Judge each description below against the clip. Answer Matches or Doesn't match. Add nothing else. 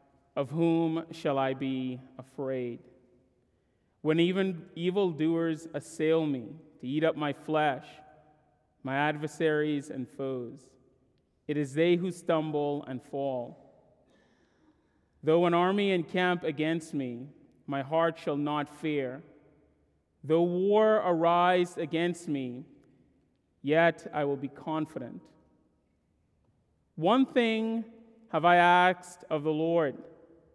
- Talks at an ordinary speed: Doesn't match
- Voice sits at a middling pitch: Matches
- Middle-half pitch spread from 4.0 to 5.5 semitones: Doesn't match